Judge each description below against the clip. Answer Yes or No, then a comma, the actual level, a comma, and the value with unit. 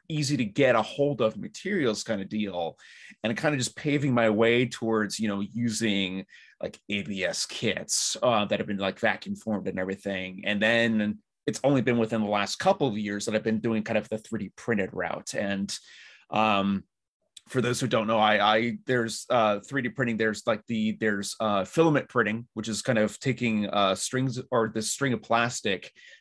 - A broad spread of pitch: No, average, 3.4 semitones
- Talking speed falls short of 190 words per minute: No, average, 195 wpm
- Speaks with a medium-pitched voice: No, low, 110 Hz